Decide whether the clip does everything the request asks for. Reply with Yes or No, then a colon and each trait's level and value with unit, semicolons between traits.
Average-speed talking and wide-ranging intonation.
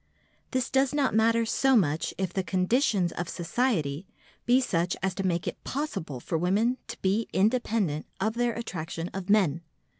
Yes: average, 170 wpm; wide, 5.7 semitones